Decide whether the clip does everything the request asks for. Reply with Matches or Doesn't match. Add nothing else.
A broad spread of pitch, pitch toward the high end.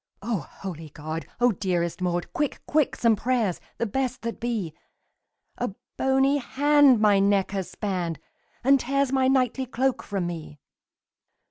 Matches